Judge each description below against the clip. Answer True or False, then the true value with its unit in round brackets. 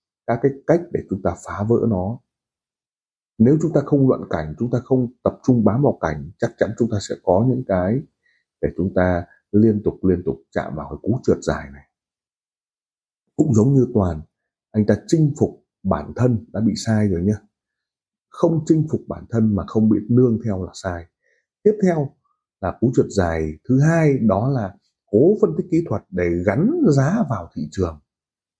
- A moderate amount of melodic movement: False (6.9 semitones)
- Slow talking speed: False (195 wpm)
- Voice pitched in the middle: False (110 Hz)